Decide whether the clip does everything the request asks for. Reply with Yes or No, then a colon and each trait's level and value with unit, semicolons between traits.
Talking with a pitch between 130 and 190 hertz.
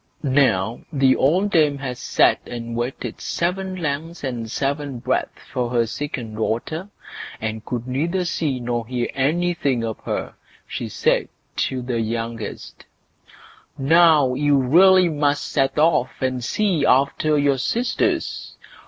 Yes: low, 135 Hz